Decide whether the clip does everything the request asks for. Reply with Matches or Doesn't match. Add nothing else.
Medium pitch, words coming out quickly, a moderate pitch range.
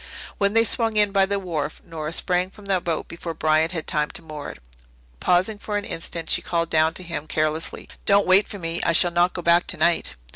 Matches